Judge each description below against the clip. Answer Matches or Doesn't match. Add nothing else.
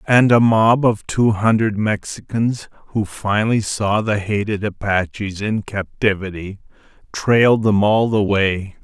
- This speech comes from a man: Matches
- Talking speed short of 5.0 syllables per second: Matches